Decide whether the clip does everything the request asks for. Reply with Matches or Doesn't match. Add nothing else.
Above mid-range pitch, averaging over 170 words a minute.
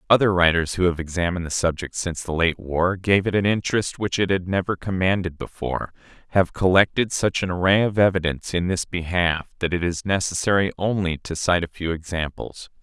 Doesn't match